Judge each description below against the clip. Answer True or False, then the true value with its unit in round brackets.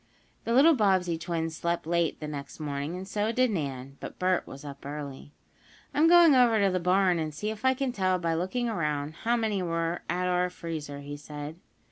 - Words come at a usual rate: False (210 wpm)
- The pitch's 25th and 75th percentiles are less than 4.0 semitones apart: False (5.6 semitones)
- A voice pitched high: False (175 Hz)